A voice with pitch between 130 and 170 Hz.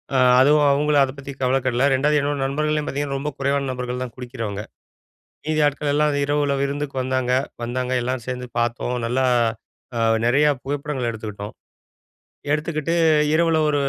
Yes: medium, 140 Hz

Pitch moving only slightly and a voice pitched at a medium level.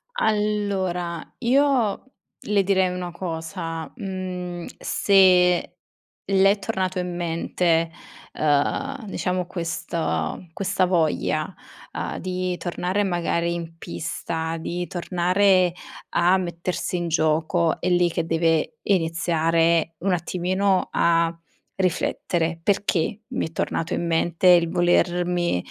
Yes: narrow, 2.1 semitones; medium, 175 Hz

